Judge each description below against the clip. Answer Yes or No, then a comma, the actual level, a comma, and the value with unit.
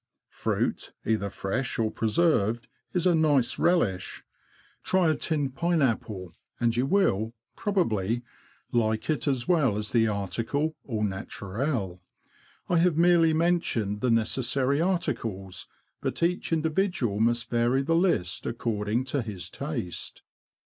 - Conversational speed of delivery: No, slow, 130 wpm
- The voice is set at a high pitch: No, low, 120 Hz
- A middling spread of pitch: No, wide, 7.0 semitones